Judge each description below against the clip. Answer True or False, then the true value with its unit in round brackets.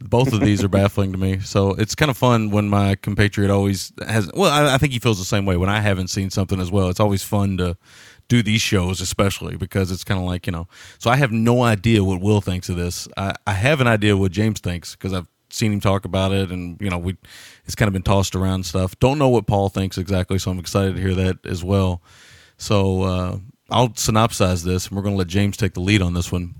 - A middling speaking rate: False (260 wpm)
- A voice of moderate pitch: False (100 Hz)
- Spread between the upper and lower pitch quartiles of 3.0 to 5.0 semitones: False (2.4 semitones)